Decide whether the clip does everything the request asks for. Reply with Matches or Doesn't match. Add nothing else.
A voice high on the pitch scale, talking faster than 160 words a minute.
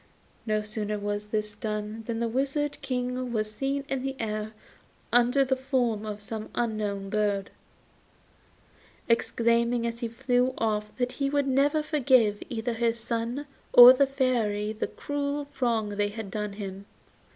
Doesn't match